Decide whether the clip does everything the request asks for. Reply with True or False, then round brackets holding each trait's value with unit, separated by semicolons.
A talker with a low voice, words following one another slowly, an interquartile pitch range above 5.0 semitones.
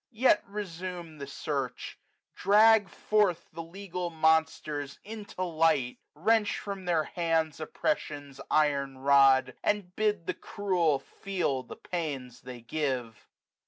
False (165 Hz; 125 wpm; 5.6 semitones)